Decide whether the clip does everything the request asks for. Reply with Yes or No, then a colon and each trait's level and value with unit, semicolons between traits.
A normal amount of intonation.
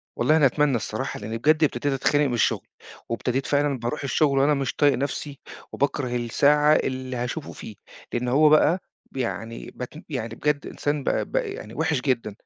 Yes: average, 3.3 semitones